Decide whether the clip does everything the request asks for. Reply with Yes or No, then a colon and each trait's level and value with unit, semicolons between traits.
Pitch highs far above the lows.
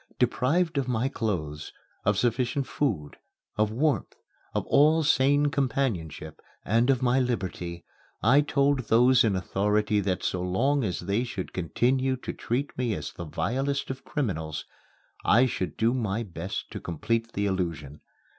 Yes: wide, 6.0 semitones